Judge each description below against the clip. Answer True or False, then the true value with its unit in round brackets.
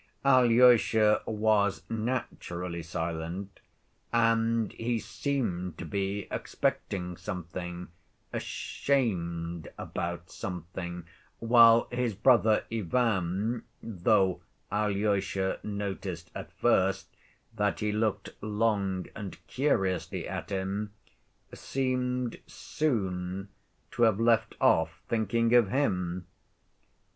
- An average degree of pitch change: True (4.1 semitones)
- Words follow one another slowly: True (90 wpm)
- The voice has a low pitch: True (100 Hz)